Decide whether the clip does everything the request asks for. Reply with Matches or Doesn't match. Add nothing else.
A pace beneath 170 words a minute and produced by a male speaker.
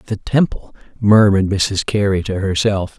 Matches